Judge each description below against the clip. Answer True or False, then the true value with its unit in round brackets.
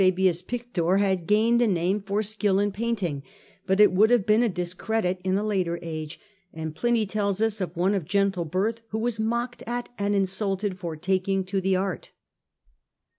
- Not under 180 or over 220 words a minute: True (190 wpm)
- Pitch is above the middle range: True (195 Hz)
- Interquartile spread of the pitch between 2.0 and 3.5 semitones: True (2.9 semitones)